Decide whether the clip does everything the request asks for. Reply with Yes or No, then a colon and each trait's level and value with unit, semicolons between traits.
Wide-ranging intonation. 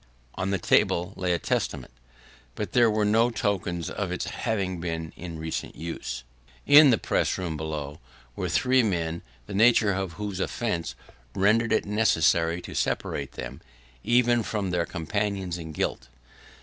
No: average, 4.5 semitones